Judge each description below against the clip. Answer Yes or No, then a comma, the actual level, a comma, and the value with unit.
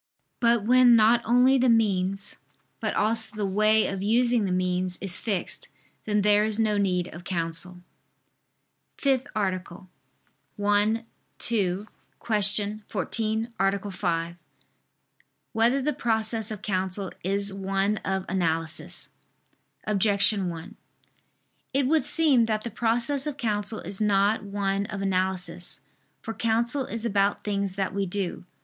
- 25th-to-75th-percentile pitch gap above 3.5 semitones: No, average, 3.0 semitones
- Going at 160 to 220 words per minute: No, slow, 135 wpm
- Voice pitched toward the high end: Yes, high, 205 Hz